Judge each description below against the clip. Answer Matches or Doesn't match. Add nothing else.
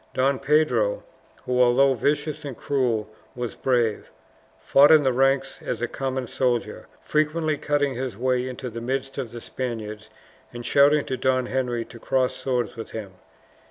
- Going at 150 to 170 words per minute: Matches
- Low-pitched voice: Matches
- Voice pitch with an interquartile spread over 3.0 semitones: Doesn't match